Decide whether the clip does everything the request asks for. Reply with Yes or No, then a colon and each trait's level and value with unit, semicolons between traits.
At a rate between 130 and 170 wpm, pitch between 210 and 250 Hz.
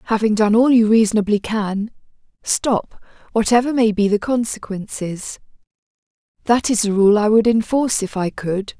Yes: average, 150 wpm; high, 215 Hz